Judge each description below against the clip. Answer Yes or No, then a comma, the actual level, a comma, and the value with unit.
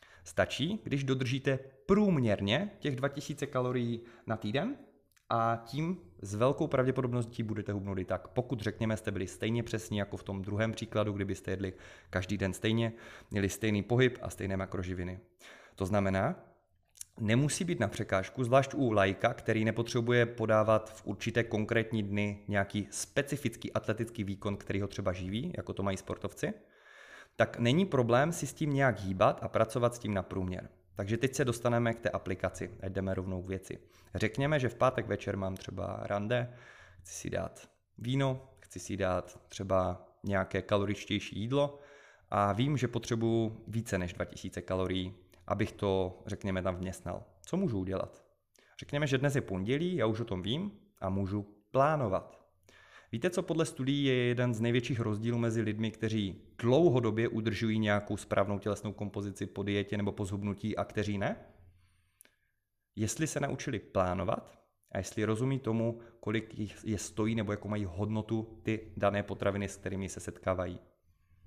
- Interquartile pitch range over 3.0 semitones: Yes, average, 3.8 semitones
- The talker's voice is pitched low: Yes, low, 105 Hz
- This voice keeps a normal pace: Yes, average, 160 wpm